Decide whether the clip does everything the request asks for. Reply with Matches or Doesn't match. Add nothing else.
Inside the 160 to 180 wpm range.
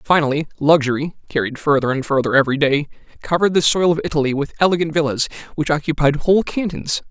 Matches